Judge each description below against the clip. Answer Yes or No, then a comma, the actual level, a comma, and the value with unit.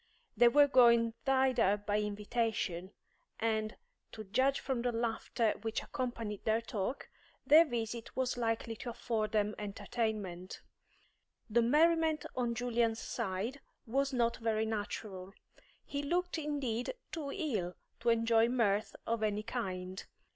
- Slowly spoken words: Yes, slow, 130 wpm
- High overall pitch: Yes, high, 230 Hz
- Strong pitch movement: No, average, 3.1 semitones